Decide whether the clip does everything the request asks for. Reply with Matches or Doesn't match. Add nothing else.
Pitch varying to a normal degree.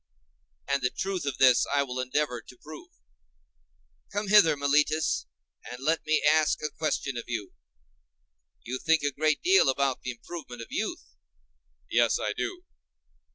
Doesn't match